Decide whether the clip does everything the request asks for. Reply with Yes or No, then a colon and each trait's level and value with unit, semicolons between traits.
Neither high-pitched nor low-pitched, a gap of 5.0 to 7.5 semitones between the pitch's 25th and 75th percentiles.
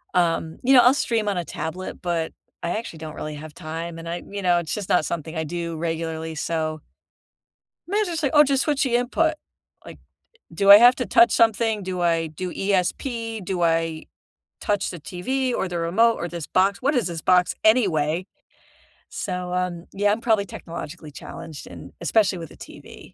Yes: medium, 180 Hz; average, 5.3 semitones